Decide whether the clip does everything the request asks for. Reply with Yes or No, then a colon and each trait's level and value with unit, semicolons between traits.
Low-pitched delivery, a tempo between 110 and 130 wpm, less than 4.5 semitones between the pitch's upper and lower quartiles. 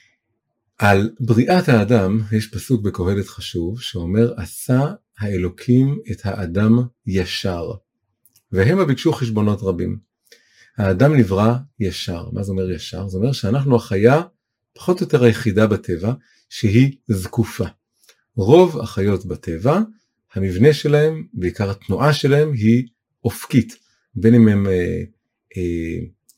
Yes: low, 115 Hz; average, 115 wpm; average, 3.7 semitones